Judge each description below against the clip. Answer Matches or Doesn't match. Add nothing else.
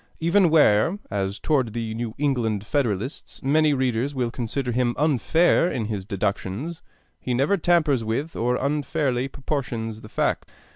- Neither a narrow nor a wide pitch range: Matches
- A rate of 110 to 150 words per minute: Matches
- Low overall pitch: Matches